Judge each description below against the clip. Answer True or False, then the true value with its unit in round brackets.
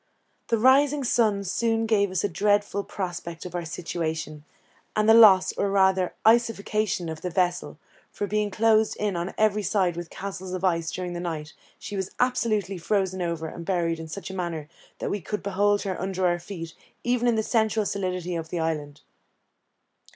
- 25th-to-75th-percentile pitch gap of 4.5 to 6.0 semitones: False (3.5 semitones)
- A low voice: False (190 Hz)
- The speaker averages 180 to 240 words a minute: True (185 wpm)